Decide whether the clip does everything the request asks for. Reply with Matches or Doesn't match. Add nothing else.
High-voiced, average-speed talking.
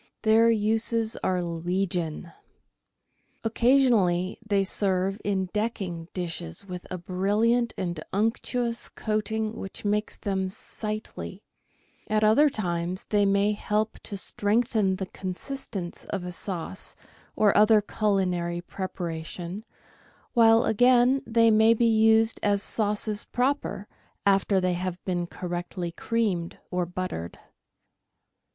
Doesn't match